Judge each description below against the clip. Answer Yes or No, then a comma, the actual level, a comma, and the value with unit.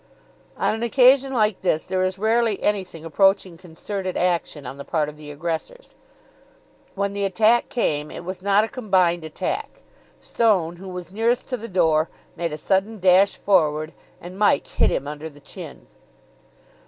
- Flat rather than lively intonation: No, average, 4.7 semitones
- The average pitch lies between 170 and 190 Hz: Yes, medium, 185 Hz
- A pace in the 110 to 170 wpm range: Yes, average, 165 wpm